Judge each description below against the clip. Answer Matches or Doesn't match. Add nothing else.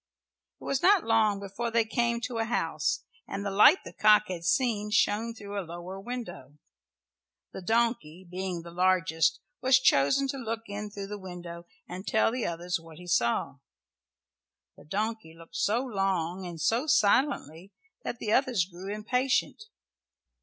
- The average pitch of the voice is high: Matches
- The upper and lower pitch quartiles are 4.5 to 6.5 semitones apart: Matches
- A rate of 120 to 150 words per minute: Doesn't match